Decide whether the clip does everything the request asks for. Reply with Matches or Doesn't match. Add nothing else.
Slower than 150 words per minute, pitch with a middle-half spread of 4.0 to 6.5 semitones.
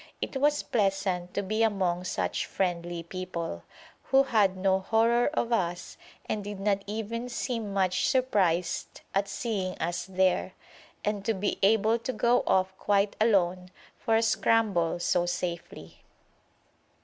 Doesn't match